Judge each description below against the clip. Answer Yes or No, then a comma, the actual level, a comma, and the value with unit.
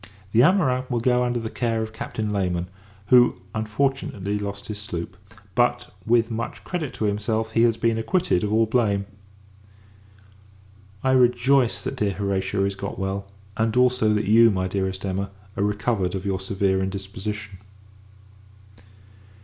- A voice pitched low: Yes, low, 110 Hz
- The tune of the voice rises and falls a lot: No, average, 3.5 semitones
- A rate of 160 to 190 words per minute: No, average, 150 wpm